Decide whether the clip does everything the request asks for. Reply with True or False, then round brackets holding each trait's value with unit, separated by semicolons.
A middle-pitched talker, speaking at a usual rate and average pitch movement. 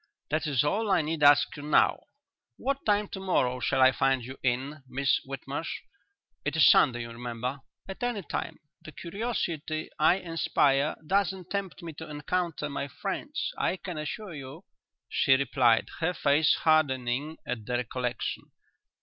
True (150 Hz; 160 wpm; 4.8 semitones)